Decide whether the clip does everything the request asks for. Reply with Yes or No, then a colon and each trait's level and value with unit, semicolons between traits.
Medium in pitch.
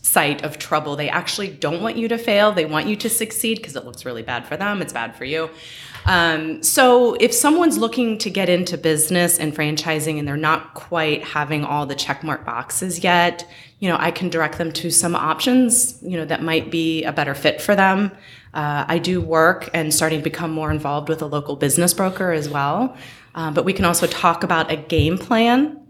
Yes: medium, 165 Hz